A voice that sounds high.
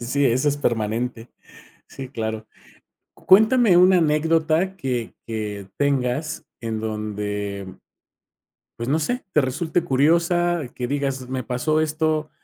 No: low, 135 Hz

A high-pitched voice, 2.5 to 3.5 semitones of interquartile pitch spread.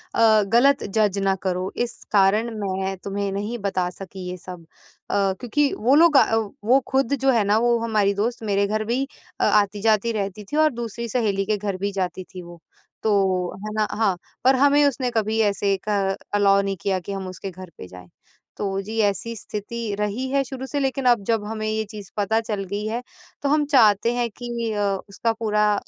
Yes: high, 210 Hz; average, 3.2 semitones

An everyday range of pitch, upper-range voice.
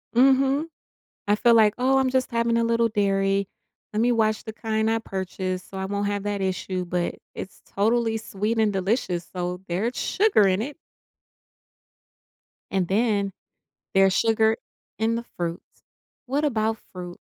Yes: average, 3.2 semitones; high, 215 Hz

